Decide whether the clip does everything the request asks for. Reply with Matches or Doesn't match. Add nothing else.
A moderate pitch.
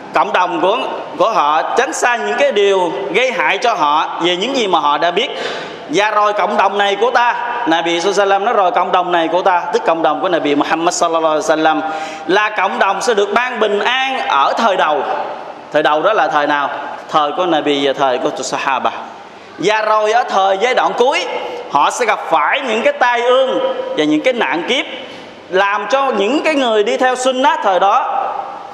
Doesn't match